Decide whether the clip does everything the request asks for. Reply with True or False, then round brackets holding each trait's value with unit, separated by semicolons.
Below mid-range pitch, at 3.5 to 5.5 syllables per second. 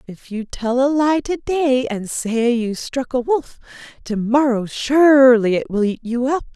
False (250 Hz; 4.1 syllables/s)